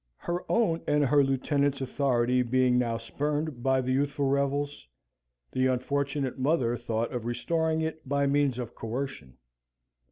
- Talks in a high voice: No, low, 135 Hz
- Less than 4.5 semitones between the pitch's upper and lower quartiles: Yes, narrow, 2.6 semitones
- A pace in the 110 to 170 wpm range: Yes, average, 140 wpm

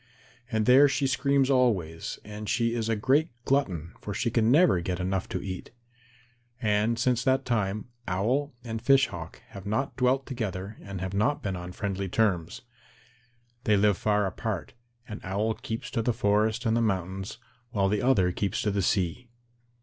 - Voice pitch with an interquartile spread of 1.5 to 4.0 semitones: No, average, 4.4 semitones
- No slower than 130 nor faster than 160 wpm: No, average, 175 wpm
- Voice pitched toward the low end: Yes, low, 110 Hz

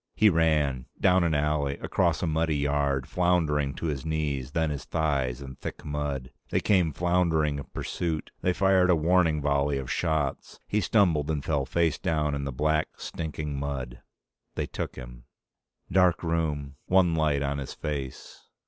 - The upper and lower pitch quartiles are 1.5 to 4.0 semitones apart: Yes, average, 2.8 semitones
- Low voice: Yes, very low, 75 Hz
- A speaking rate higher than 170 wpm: No, average, 165 wpm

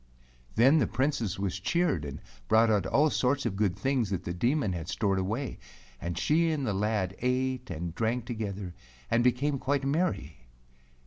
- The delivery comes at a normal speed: Yes, average, 175 wpm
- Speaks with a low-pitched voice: Yes, low, 115 Hz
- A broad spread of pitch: Yes, wide, 6.0 semitones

